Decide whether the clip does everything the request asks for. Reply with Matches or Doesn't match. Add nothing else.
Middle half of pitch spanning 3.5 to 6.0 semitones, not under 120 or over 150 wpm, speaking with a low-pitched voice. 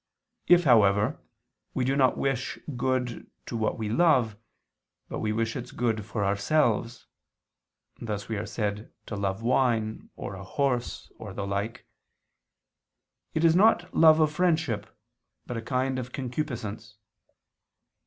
Matches